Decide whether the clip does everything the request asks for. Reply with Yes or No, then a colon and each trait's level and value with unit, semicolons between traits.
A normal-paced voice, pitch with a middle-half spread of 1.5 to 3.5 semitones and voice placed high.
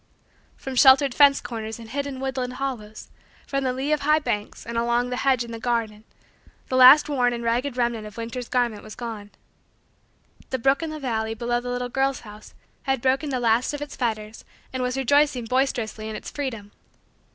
Yes: average, 195 wpm; average, 2.8 semitones; high, 245 Hz